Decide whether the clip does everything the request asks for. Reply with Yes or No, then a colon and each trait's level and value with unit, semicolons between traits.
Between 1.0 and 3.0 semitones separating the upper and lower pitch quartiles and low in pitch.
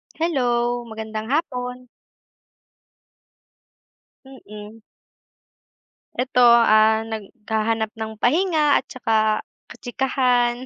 No: average, 2.7 semitones; high, 240 Hz